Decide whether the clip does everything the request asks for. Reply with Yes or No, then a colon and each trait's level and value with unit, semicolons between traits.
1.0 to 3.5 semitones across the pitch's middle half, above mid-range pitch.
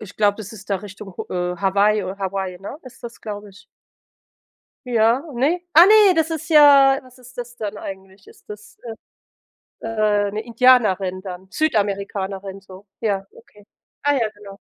No: average, 4.2 semitones; high, 210 Hz